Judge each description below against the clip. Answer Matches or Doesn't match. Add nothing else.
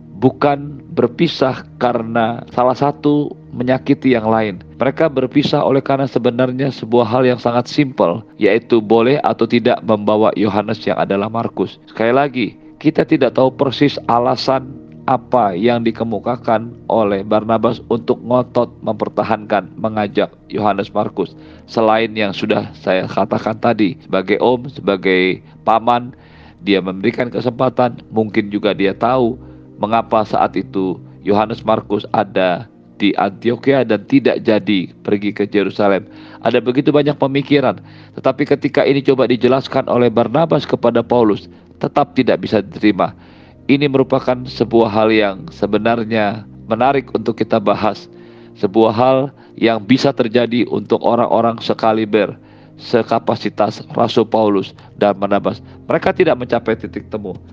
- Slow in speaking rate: Doesn't match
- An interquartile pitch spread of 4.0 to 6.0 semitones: Doesn't match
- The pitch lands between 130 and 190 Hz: Doesn't match